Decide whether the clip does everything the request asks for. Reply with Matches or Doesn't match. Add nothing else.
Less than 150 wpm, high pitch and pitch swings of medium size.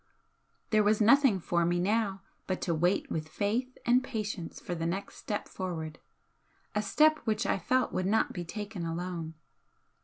Doesn't match